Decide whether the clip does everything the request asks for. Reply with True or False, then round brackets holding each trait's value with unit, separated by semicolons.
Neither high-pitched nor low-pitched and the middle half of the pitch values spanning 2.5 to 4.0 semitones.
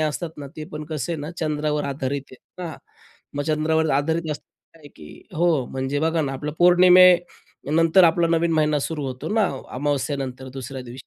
True (150 Hz; 2.8 semitones)